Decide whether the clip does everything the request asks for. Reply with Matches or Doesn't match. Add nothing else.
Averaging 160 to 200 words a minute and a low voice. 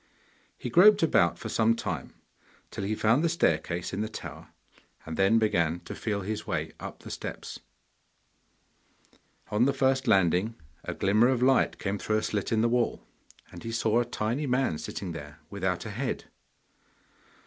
Matches